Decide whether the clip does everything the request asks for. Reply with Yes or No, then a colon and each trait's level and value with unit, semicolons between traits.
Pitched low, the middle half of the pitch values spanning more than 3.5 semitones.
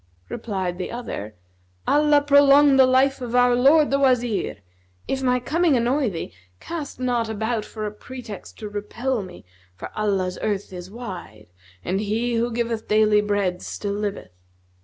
No: high, 230 Hz; average, 4.3 semitones